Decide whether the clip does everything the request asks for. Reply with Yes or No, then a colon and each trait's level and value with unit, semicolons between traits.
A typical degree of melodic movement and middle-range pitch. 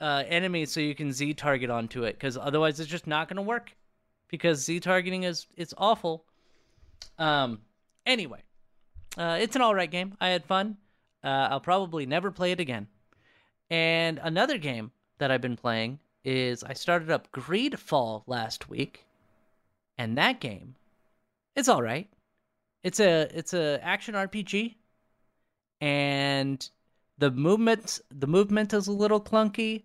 No: wide, 5.8 semitones; medium, 160 Hz